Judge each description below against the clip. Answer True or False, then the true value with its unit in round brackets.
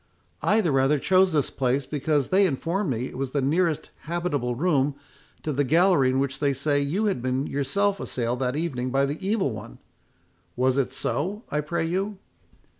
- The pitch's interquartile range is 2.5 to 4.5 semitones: False (4.9 semitones)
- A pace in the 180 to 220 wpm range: True (185 wpm)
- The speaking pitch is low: False (145 Hz)